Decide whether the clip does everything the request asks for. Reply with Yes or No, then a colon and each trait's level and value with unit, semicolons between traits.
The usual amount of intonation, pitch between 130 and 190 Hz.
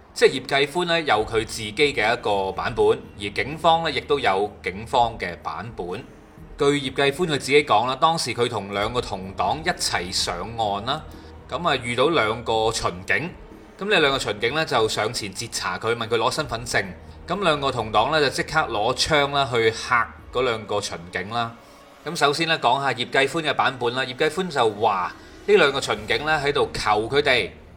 No: wide, 6.0 semitones; medium, 140 Hz